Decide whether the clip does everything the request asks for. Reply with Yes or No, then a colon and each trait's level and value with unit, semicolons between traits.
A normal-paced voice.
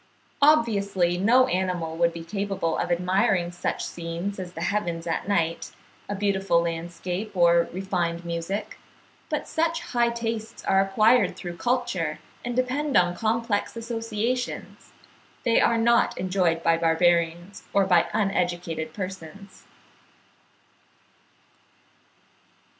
No: slow, 115 wpm